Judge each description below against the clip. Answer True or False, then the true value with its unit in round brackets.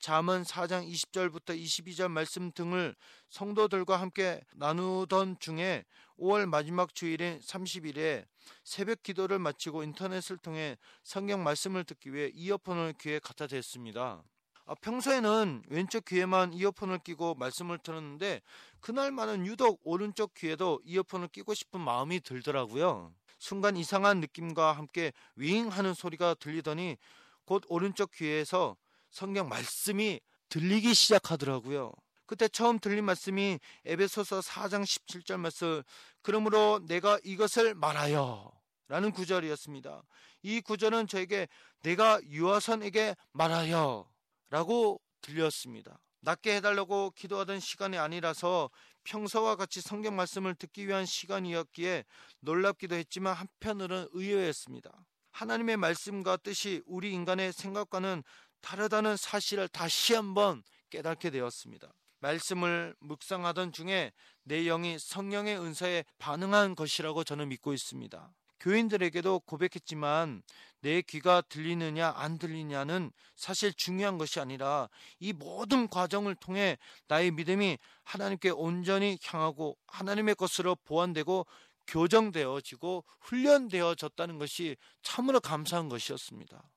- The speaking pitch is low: False (180 Hz)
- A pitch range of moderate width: True (3.9 semitones)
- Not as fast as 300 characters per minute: False (305 characters per minute)